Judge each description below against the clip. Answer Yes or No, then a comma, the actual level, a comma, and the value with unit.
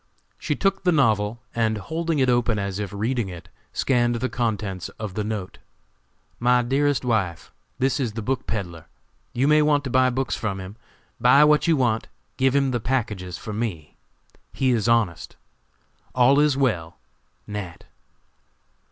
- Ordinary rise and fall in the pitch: Yes, average, 4.4 semitones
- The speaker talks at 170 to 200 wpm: No, average, 160 wpm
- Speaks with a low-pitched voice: Yes, low, 120 Hz